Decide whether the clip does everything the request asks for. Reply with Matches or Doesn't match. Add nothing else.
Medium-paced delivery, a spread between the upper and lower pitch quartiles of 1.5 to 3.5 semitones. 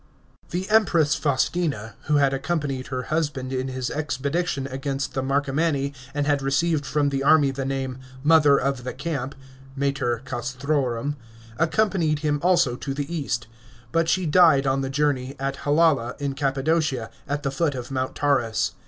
Matches